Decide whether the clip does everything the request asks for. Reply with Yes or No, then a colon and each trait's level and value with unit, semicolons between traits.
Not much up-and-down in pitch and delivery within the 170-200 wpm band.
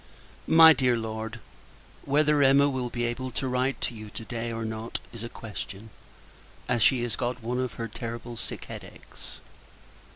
Yes: narrow, 2.3 semitones; average, 175 wpm